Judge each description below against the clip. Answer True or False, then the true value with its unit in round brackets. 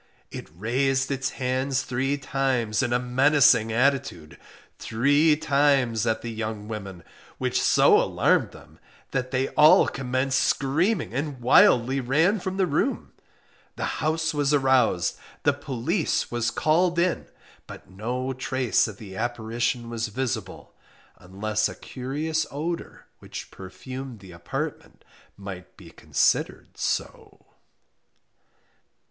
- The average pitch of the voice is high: False (130 Hz)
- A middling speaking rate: False (125 wpm)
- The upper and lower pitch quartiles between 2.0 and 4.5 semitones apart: True (4.0 semitones)